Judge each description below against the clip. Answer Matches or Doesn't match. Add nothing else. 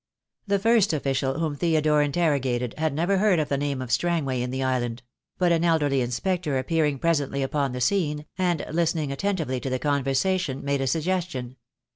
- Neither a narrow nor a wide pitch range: Matches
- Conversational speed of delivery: Matches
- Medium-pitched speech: Matches